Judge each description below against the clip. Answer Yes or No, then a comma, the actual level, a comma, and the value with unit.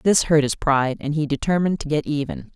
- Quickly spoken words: Yes, fast, 235 wpm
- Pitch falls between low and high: Yes, medium, 150 Hz